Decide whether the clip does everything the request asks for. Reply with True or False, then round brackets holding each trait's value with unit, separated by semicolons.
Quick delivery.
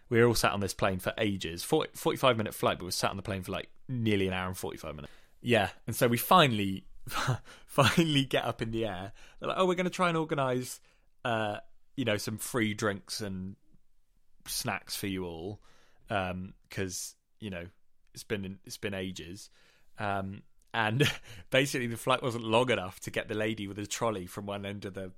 True (210 wpm)